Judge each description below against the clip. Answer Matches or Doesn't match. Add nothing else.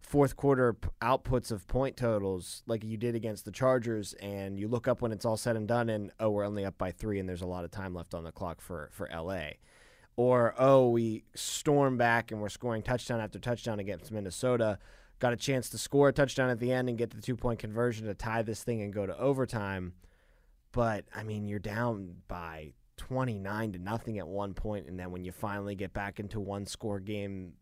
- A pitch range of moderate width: Matches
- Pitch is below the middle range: Matches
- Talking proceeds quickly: Matches